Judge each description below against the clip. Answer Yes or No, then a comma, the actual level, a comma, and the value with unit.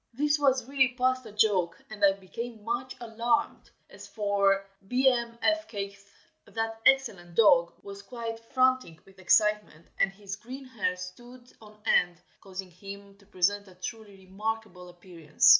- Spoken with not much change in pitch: No, average, 3.9 semitones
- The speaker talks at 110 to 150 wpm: Yes, average, 140 wpm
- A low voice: No, high, 210 Hz